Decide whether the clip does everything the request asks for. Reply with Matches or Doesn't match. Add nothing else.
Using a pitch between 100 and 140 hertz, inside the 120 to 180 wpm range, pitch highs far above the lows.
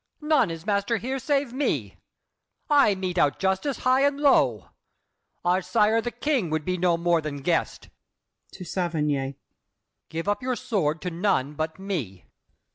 Doesn't match